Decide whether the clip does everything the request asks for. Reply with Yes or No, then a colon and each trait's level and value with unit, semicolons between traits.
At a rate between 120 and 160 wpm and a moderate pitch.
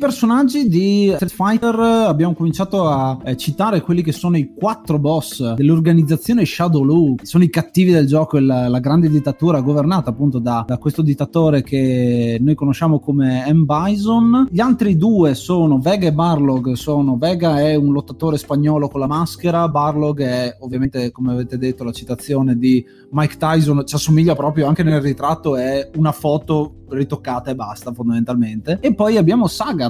No: fast, 170 wpm; medium, 150 Hz